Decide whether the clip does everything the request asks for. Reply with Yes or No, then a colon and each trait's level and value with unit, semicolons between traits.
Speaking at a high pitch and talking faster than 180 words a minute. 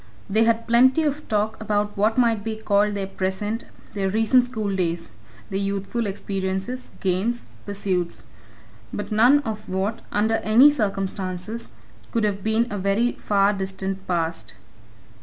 No: high, 210 Hz; average, 140 wpm